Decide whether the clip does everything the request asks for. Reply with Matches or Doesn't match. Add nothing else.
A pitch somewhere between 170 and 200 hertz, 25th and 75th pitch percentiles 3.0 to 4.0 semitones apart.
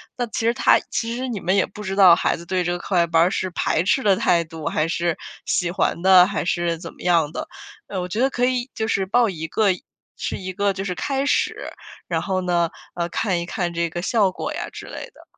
Matches